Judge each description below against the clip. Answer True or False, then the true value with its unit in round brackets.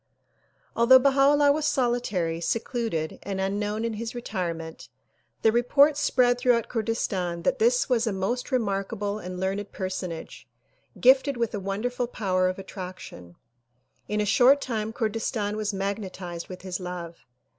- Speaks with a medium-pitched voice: False (210 Hz)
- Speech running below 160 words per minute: True (135 wpm)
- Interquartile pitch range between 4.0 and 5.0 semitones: True (4.6 semitones)